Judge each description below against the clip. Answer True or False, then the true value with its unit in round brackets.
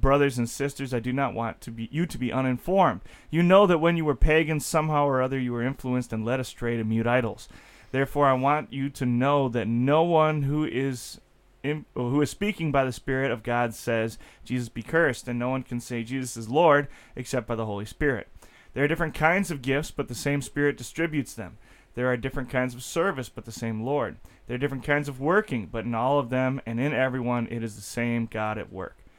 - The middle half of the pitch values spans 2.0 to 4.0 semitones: True (3.5 semitones)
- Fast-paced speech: True (230 wpm)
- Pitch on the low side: True (130 Hz)